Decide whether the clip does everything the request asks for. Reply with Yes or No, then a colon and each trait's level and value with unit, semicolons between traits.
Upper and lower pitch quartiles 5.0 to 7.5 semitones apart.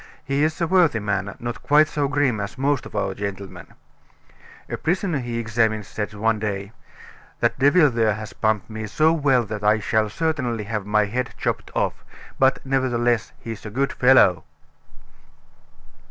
No: average, 4.6 semitones